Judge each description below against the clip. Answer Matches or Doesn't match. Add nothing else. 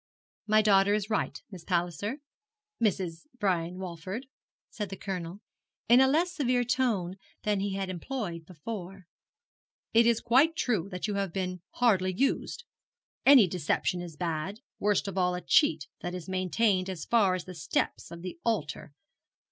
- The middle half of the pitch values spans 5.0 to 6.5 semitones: Doesn't match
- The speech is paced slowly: Doesn't match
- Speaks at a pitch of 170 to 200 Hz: Matches